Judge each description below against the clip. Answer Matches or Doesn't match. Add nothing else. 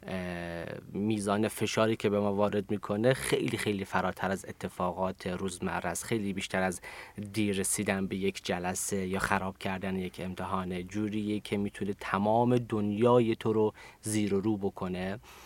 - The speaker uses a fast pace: Doesn't match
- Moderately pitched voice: Doesn't match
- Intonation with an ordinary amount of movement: Doesn't match